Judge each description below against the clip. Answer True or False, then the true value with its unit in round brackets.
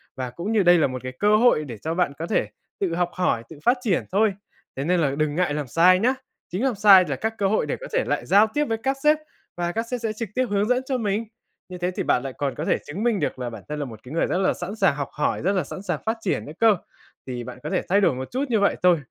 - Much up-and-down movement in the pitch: True (6.8 semitones)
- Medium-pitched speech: True (180 Hz)